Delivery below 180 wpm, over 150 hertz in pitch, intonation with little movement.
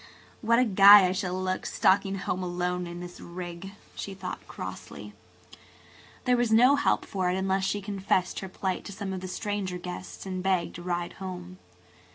No: average, 185 wpm; high, 190 Hz; narrow, 1.8 semitones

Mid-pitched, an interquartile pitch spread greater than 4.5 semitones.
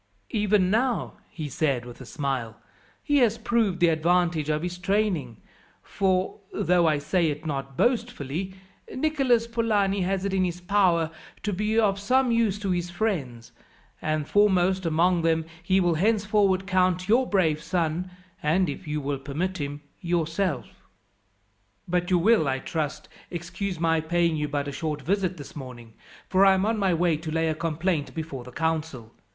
No: medium, 175 Hz; average, 4.2 semitones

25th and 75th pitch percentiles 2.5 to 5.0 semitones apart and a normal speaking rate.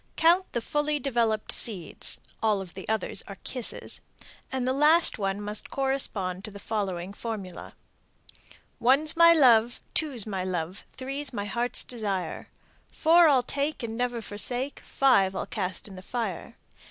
No: wide, 5.5 semitones; average, 155 wpm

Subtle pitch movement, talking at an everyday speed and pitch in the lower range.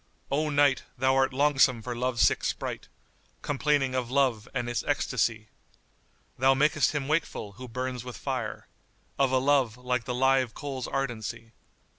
Yes: narrow, 2.2 semitones; average, 165 wpm; low, 130 Hz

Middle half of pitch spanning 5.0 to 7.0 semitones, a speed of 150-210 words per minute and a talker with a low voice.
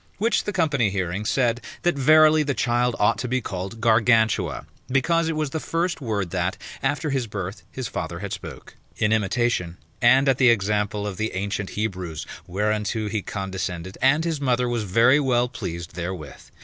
Yes: wide, 5.4 semitones; average, 175 wpm; low, 115 Hz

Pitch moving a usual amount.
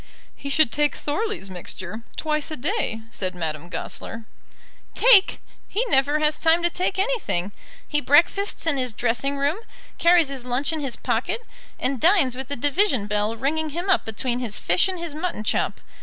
No: wide, 6.5 semitones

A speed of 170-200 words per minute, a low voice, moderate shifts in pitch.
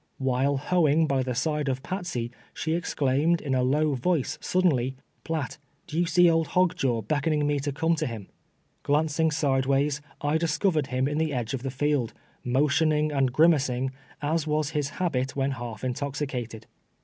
No: average, 175 wpm; medium, 145 Hz; average, 3.3 semitones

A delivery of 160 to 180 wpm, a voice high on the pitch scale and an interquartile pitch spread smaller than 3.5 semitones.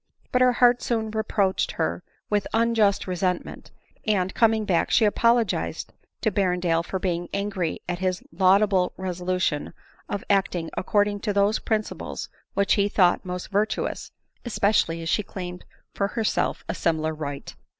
No: average, 150 wpm; high, 195 Hz; average, 3.0 semitones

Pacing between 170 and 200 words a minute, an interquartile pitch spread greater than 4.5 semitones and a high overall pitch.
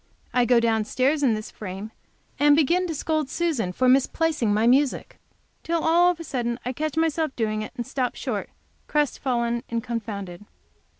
Yes: average, 175 wpm; average, 5.3 semitones; very high, 255 Hz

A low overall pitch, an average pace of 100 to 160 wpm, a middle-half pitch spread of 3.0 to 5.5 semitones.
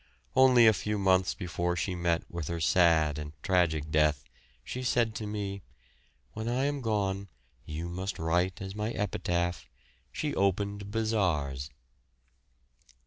Yes: very low, 95 Hz; average, 140 wpm; average, 4.1 semitones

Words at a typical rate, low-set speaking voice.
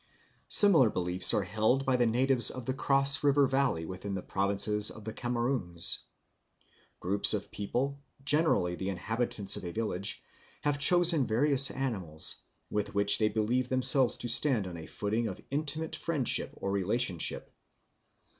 Yes: average, 150 wpm; low, 115 Hz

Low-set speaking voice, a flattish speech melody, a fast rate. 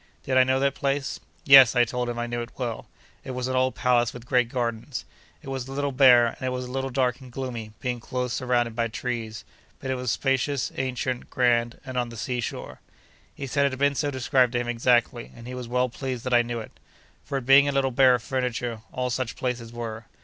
Yes: low, 125 Hz; narrow, 1.7 semitones; fast, 235 wpm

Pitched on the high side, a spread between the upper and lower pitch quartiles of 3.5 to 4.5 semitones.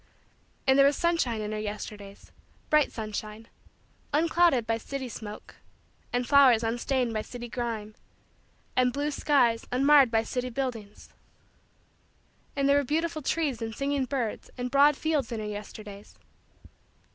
Yes: high, 245 Hz; average, 4.1 semitones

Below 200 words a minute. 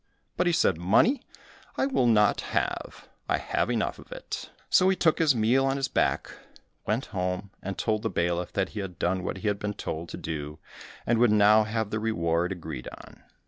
No: fast, 205 wpm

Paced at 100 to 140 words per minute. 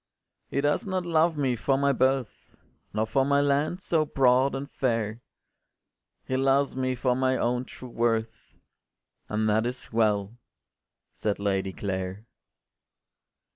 Yes: slow, 135 wpm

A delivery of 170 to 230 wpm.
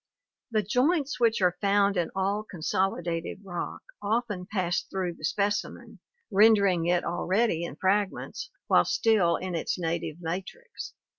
No: slow, 135 wpm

